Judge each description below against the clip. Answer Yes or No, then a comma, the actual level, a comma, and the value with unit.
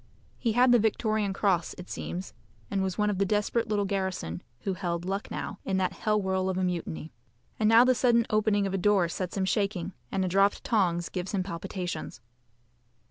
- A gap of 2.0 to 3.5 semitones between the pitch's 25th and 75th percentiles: Yes, narrow, 2.5 semitones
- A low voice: No, high, 195 Hz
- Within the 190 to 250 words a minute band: Yes, average, 195 wpm